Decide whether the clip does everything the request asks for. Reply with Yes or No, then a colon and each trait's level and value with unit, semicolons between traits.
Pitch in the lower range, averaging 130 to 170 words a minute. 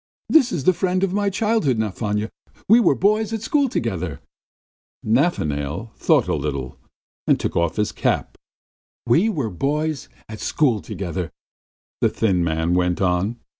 Yes: low, 115 Hz; average, 150 wpm